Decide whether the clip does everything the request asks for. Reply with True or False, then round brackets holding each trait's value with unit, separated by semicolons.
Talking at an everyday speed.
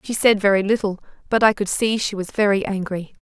False (225 wpm)